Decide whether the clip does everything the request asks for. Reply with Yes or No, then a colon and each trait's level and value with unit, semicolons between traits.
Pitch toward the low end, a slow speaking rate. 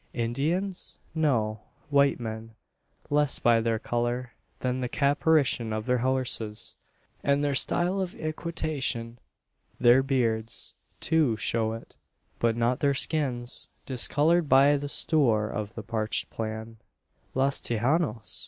Yes: low, 125 Hz; slow, 125 wpm